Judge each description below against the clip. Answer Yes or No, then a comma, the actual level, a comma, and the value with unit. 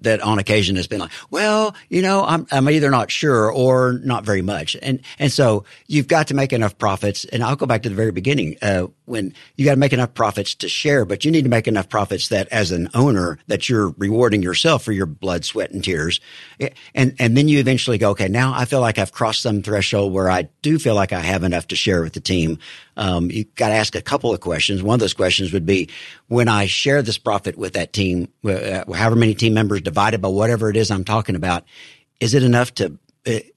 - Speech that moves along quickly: Yes, fast, 240 wpm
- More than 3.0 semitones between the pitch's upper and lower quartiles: Yes, average, 5.0 semitones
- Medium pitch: No, low, 110 Hz